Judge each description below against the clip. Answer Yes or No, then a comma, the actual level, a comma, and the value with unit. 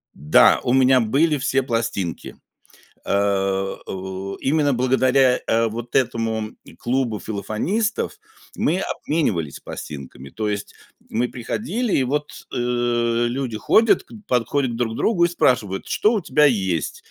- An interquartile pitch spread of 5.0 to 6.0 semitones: Yes, average, 5.3 semitones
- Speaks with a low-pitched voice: Yes, low, 120 Hz